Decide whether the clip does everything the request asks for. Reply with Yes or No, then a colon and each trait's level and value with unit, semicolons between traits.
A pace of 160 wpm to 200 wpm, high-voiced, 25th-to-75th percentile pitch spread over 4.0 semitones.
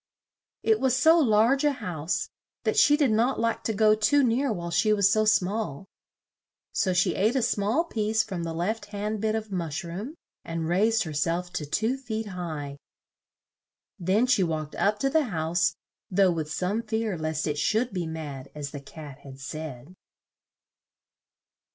Yes: average, 175 wpm; high, 200 Hz; wide, 5.6 semitones